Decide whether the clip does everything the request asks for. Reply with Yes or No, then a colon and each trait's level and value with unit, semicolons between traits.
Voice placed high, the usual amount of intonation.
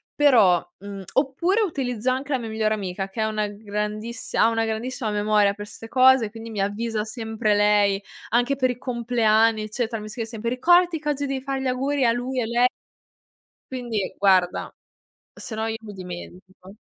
Yes: high, 225 Hz; average, 3.4 semitones